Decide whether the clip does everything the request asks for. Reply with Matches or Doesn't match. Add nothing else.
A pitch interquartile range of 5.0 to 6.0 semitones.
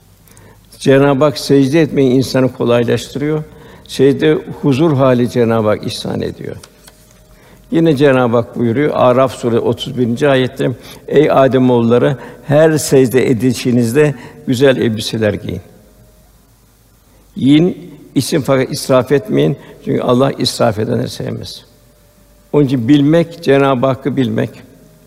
Doesn't match